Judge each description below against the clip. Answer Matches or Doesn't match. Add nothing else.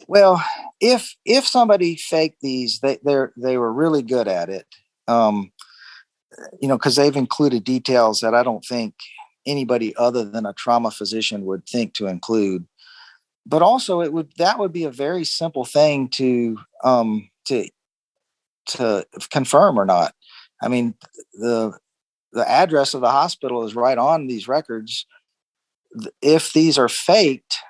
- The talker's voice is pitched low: Matches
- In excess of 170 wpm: Doesn't match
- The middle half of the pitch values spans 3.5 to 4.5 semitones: Doesn't match